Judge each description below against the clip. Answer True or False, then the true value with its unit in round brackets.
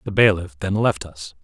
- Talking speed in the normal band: False (210 wpm)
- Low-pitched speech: True (95 Hz)